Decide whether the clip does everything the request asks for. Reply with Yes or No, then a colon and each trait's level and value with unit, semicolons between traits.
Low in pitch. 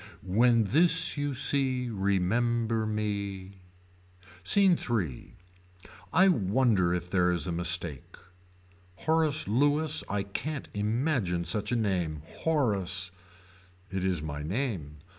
Yes: low, 105 Hz